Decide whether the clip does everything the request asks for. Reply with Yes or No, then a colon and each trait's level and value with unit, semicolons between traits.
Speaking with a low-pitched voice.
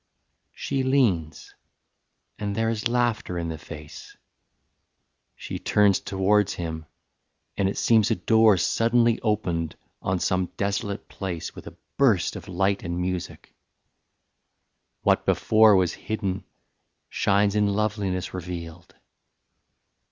Yes: low, 100 Hz